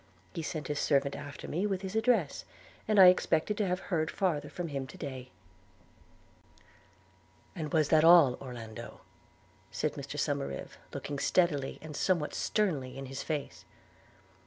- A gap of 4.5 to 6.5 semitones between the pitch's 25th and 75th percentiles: Yes, average, 4.8 semitones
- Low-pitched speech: No, medium, 155 Hz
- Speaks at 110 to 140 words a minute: No, average, 150 wpm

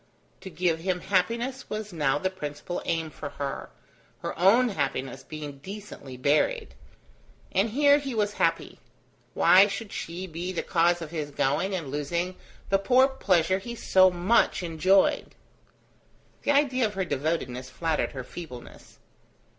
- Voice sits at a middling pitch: Yes, medium, 180 Hz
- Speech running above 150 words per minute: No, average, 145 wpm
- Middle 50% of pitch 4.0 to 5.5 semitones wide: Yes, average, 5.2 semitones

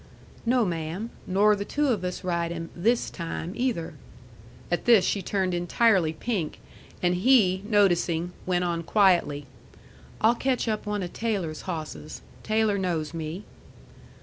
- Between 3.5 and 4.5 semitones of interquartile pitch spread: Yes, average, 4.2 semitones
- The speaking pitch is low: No, medium, 185 Hz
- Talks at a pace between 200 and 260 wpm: No, average, 145 wpm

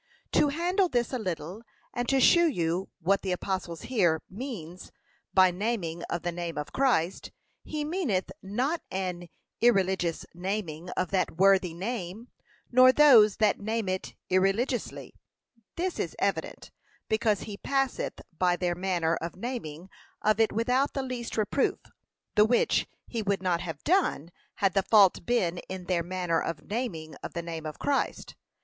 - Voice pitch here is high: Yes, high, 195 Hz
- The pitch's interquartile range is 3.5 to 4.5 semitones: No, wide, 5.6 semitones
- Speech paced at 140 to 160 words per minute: Yes, average, 155 wpm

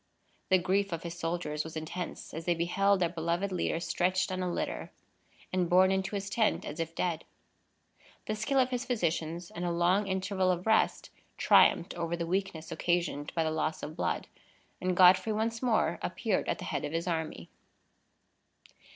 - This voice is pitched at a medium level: Yes, medium, 180 Hz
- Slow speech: No, average, 180 wpm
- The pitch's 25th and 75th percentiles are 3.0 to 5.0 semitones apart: No, narrow, 2.6 semitones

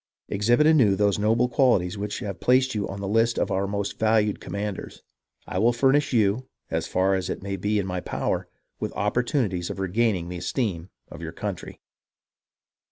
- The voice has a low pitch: Yes, low, 105 Hz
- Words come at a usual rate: Yes, average, 180 wpm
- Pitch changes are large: No, average, 3.6 semitones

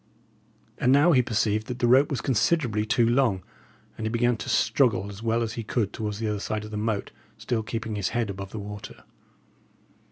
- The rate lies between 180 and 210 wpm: Yes, average, 200 wpm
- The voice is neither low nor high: No, low, 110 Hz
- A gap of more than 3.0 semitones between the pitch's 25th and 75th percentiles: No, narrow, 2.4 semitones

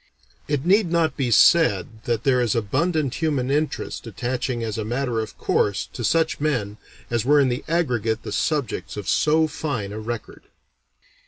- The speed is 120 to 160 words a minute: No, average, 170 wpm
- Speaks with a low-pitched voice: Yes, low, 125 Hz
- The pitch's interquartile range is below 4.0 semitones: No, wide, 5.4 semitones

